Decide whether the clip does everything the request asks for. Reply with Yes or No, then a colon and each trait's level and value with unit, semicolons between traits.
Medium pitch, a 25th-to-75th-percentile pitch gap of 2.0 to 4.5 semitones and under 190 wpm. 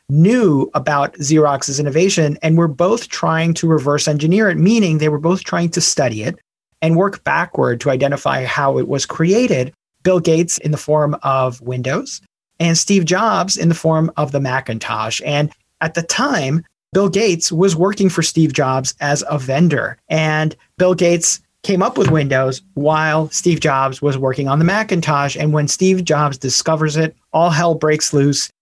Yes: medium, 155 Hz; average, 3.3 semitones; average, 175 wpm